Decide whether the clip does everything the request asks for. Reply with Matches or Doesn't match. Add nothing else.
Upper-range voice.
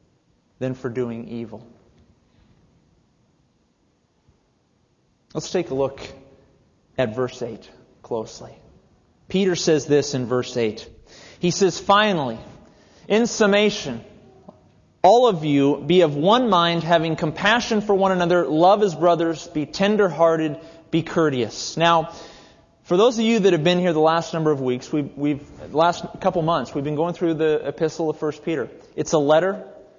Doesn't match